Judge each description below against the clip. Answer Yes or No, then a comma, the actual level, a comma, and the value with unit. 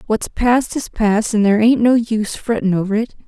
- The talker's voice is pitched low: No, high, 220 Hz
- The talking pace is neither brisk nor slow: No, fast, 220 wpm